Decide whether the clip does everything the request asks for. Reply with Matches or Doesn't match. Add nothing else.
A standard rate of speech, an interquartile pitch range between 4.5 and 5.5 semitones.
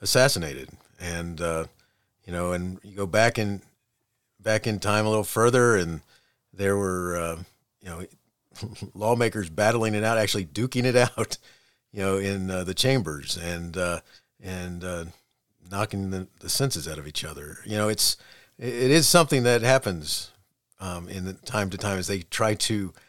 Doesn't match